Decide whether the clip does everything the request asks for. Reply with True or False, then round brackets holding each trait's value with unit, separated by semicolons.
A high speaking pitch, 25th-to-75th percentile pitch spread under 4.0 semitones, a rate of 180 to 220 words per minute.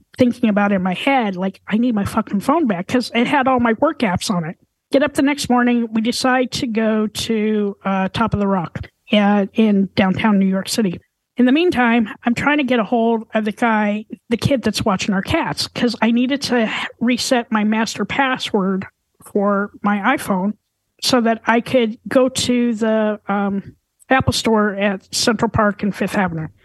True (225 Hz; 3.3 semitones; 200 wpm)